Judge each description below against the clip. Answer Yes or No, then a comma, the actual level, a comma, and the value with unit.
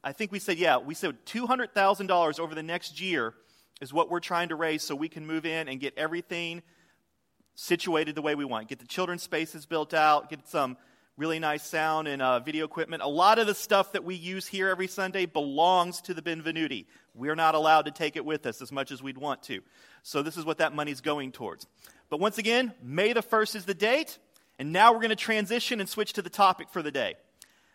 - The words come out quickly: Yes, fast, 230 wpm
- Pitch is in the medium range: Yes, medium, 165 Hz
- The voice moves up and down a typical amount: Yes, average, 4.0 semitones